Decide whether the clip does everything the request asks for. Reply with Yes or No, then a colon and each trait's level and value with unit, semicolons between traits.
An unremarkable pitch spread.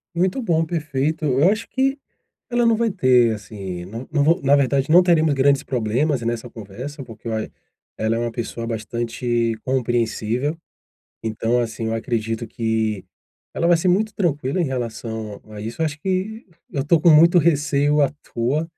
No: wide, 6.1 semitones